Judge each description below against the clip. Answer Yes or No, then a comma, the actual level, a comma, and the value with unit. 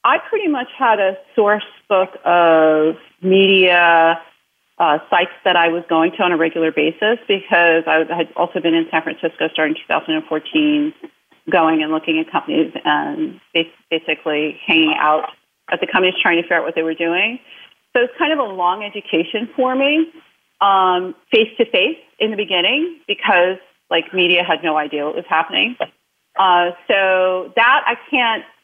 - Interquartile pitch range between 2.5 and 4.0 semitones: No, average, 5.0 semitones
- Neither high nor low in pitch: Yes, medium, 180 Hz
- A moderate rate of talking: Yes, average, 170 wpm